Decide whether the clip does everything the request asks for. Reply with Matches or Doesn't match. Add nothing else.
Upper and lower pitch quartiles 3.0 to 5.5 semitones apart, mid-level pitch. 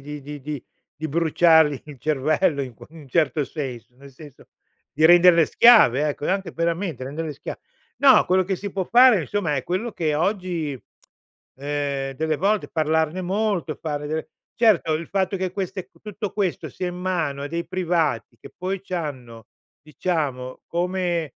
Matches